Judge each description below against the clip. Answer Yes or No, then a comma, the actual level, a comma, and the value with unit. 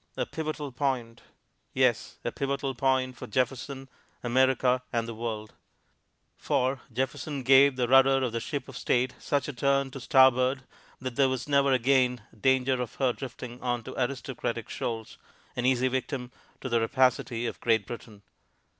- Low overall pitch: Yes, low, 130 Hz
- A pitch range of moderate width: No, narrow, 1.8 semitones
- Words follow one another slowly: No, average, 160 wpm